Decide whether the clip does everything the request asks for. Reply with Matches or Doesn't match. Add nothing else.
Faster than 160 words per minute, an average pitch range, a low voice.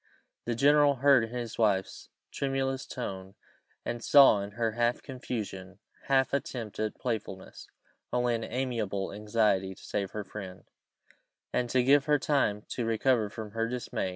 Doesn't match